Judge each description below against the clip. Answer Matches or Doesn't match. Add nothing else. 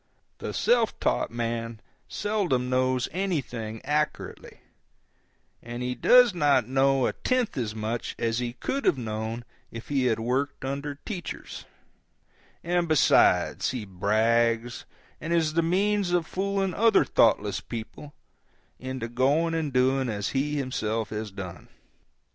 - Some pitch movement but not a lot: Doesn't match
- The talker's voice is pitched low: Matches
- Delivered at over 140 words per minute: Doesn't match